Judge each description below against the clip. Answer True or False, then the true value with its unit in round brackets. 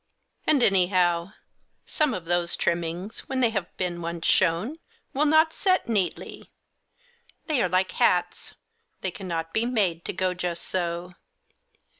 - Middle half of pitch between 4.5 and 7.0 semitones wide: True (5.1 semitones)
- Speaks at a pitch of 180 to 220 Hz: True (185 Hz)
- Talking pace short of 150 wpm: True (140 wpm)